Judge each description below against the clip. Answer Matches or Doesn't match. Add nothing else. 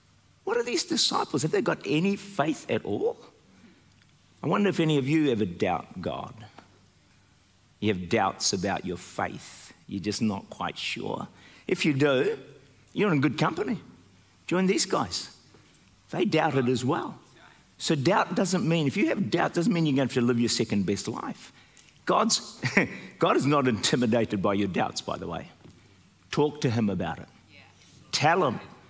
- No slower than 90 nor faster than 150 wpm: Doesn't match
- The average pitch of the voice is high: Doesn't match